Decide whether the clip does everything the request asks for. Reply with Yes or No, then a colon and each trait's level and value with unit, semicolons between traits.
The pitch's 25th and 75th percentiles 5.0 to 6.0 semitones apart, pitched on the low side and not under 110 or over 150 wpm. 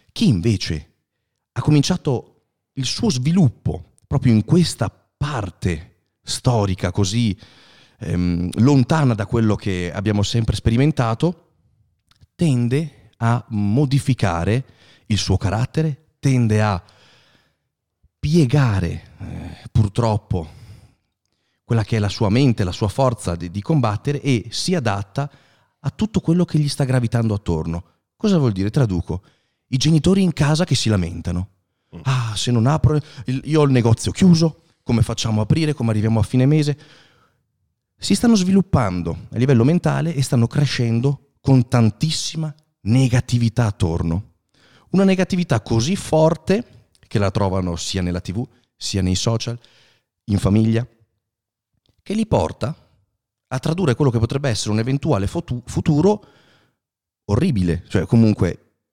Yes: average, 5.3 semitones; low, 115 Hz; average, 130 wpm